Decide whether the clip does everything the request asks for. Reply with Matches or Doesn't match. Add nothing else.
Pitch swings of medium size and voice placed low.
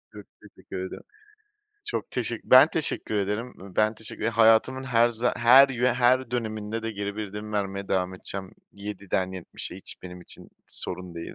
Matches